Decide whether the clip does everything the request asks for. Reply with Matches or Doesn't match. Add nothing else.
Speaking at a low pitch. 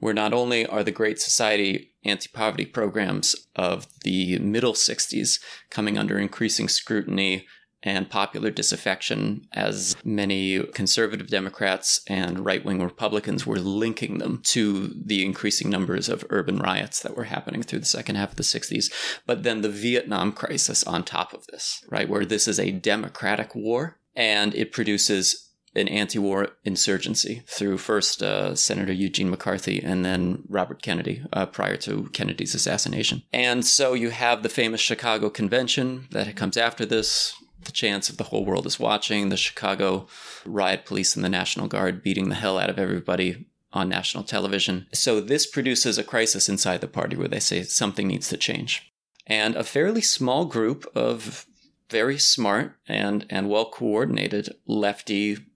Matches